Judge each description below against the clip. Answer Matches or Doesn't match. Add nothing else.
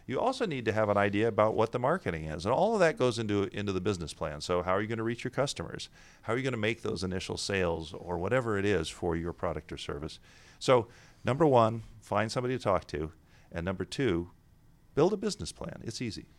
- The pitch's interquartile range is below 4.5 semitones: Doesn't match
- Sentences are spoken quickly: Matches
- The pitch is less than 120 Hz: Matches